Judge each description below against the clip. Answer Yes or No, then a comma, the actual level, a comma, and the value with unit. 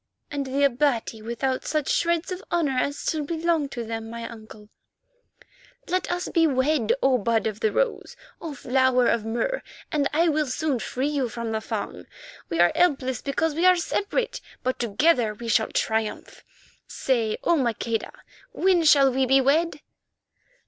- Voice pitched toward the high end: Yes, very high, 265 Hz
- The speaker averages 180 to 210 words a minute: No, average, 165 wpm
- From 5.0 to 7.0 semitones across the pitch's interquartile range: Yes, wide, 5.4 semitones